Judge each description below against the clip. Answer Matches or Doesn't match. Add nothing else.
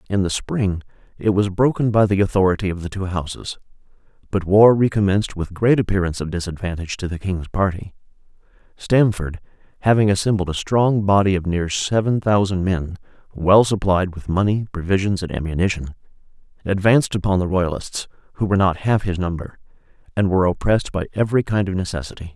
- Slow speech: Doesn't match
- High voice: Doesn't match